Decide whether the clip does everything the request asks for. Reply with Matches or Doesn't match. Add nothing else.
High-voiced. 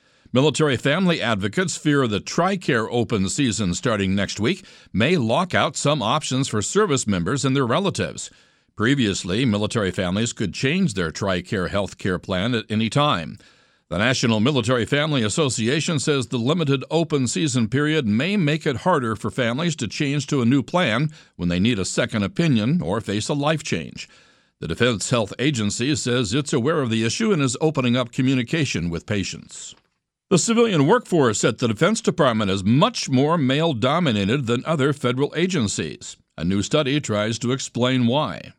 Doesn't match